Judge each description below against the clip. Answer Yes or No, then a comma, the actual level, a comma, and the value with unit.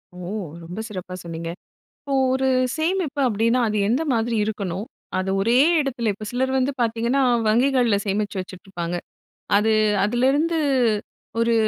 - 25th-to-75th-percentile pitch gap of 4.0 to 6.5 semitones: Yes, average, 4.6 semitones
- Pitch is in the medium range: No, high, 230 Hz